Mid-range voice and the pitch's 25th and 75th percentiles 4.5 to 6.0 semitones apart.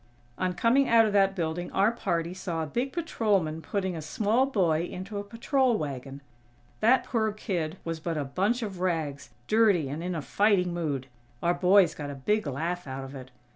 Yes: medium, 180 Hz; average, 5.2 semitones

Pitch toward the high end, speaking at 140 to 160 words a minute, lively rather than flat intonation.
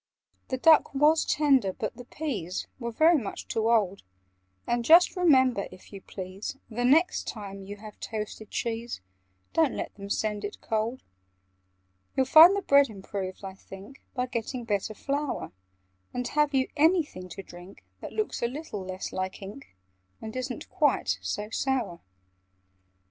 Yes: high, 235 Hz; average, 155 wpm; wide, 5.8 semitones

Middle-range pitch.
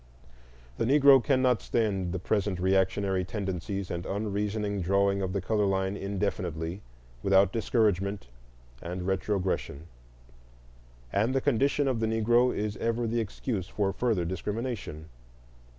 No: low, 100 Hz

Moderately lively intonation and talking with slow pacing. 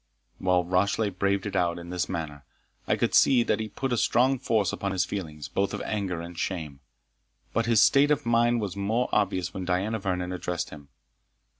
No: average, 3.9 semitones; average, 195 wpm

